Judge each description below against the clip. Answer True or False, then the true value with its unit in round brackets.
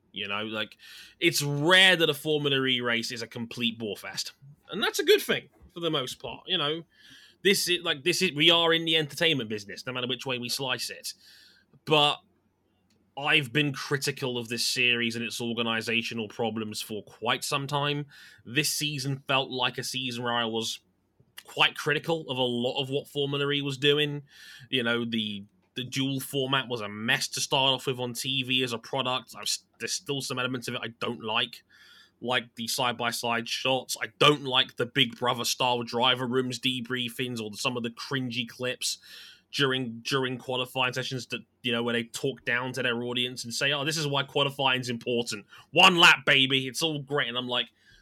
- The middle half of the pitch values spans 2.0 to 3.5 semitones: True (3.2 semitones)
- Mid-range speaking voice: False (130 Hz)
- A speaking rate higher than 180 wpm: True (200 wpm)